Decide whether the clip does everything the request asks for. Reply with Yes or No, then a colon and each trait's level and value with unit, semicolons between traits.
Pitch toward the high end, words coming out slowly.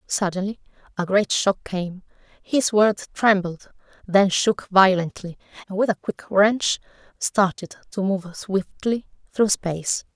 Yes: high, 195 Hz; slow, 130 wpm